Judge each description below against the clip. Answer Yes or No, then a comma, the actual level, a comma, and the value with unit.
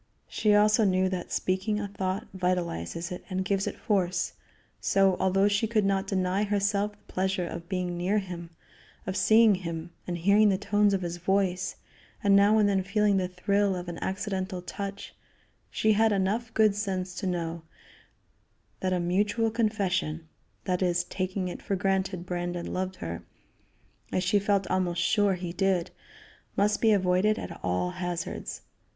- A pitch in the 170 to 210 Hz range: Yes, high, 190 Hz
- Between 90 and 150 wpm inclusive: No, average, 165 wpm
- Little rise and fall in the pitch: Yes, narrow, 2.1 semitones